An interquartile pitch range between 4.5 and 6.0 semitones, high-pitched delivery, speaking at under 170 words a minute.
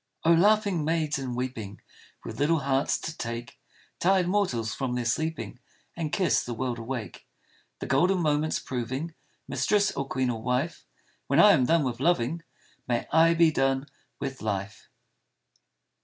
No: average, 5.1 semitones; medium, 140 Hz; average, 155 wpm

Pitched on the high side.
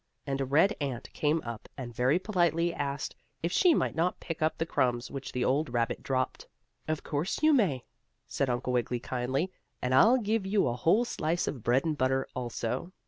No: medium, 140 Hz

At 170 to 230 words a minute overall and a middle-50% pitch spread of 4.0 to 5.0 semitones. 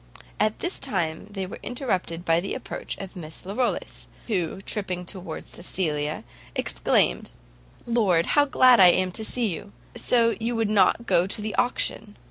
No: average, 160 wpm; average, 4.7 semitones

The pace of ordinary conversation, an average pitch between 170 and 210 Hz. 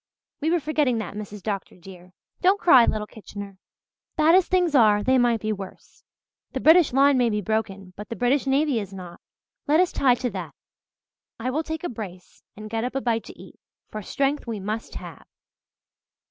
No: average, 195 wpm; high, 230 Hz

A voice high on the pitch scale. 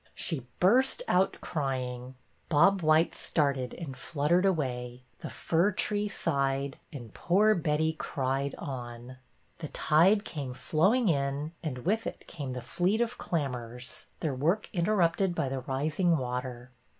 No: medium, 150 Hz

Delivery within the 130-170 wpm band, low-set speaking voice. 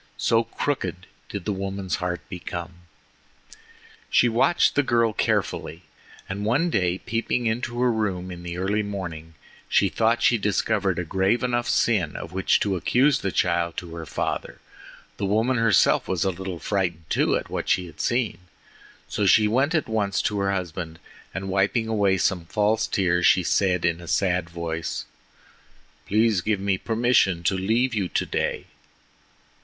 Yes: average, 165 wpm; very low, 95 Hz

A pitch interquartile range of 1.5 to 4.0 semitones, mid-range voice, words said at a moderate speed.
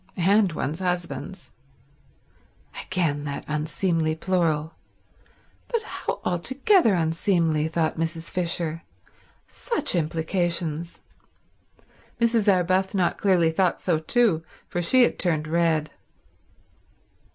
No: average, 2.9 semitones; medium, 170 Hz; slow, 95 wpm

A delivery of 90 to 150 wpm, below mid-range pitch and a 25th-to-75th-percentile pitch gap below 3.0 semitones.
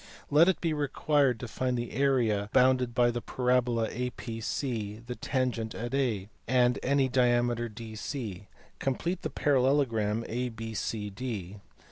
Yes: slow, 135 wpm; low, 120 Hz; narrow, 2.6 semitones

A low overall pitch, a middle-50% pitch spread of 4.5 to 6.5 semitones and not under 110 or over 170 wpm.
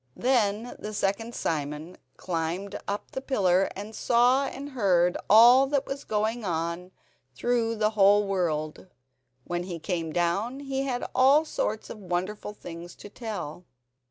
No: high, 205 Hz; wide, 5.5 semitones; average, 145 wpm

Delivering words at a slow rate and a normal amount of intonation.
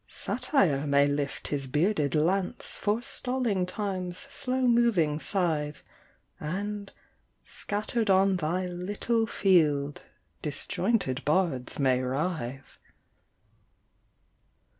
No: slow, 85 wpm; wide, 5.9 semitones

